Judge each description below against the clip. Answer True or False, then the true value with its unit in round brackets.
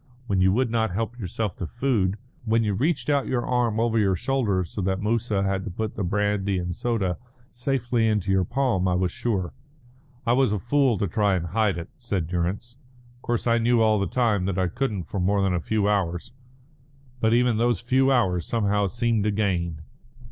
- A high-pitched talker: False (105 Hz)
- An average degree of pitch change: True (4.0 semitones)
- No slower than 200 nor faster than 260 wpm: True (205 wpm)